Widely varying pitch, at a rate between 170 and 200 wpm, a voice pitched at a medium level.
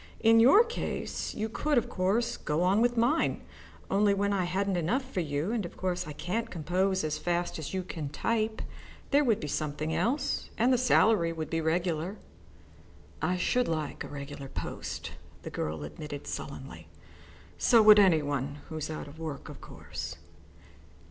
Yes: wide, 6.3 semitones; average, 175 wpm; medium, 180 Hz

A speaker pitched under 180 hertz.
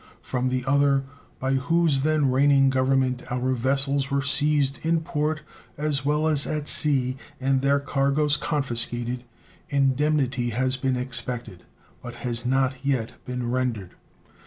Yes: low, 135 Hz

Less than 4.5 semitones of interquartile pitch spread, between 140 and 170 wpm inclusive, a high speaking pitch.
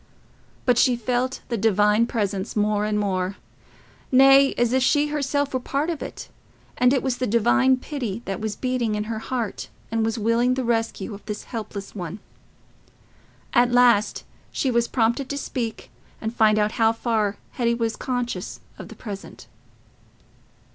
Yes: average, 3.1 semitones; average, 165 wpm; high, 235 Hz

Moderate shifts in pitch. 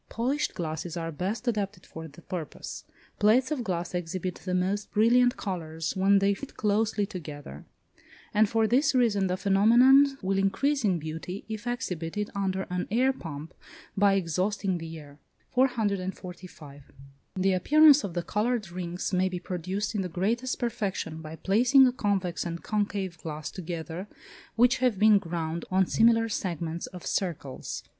Yes: average, 4.3 semitones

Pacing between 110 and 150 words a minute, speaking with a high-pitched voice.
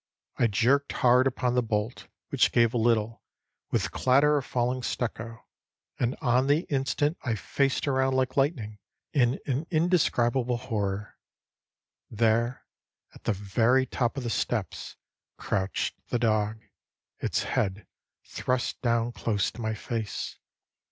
No: slow, 135 wpm; low, 120 Hz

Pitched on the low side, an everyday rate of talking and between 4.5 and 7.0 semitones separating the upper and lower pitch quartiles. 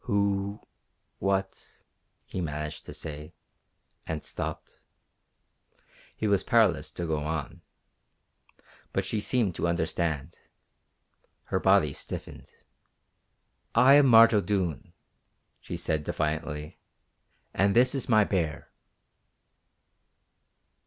No: very low, 95 Hz; slow, 100 wpm; average, 5.1 semitones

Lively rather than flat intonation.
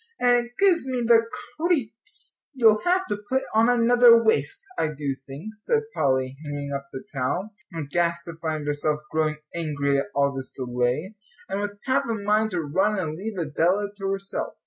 Yes: wide, 7.9 semitones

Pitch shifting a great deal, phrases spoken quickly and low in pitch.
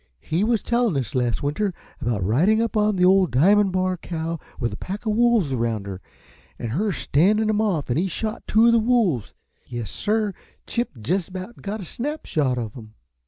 No: wide, 8.7 semitones; fast, 210 wpm; medium, 185 Hz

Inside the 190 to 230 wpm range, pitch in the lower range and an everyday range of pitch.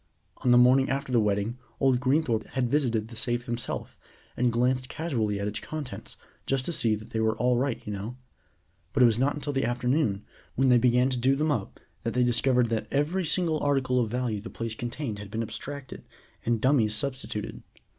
Yes: fast, 205 wpm; low, 125 Hz; average, 3.1 semitones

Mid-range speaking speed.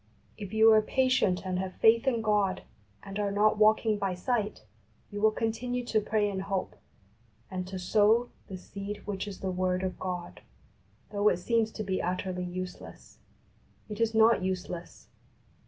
Yes: average, 170 wpm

